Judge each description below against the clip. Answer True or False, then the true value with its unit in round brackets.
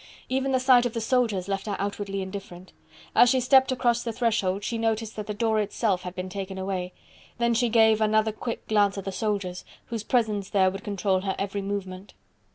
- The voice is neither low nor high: False (210 Hz)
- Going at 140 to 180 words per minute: False (205 wpm)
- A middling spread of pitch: True (3.0 semitones)